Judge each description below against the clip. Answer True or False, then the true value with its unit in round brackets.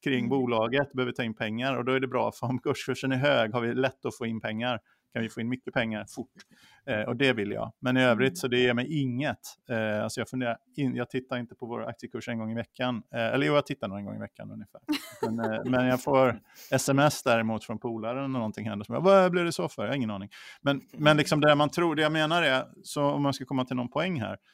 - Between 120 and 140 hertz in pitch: True (125 Hz)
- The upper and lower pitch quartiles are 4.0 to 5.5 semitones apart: False (3.6 semitones)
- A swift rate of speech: True (265 wpm)